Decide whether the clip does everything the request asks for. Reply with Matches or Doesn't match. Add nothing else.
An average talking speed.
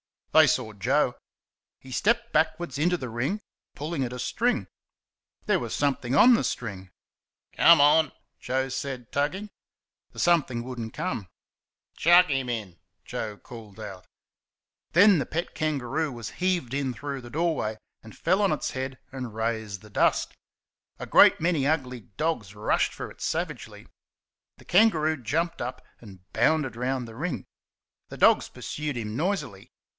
Matches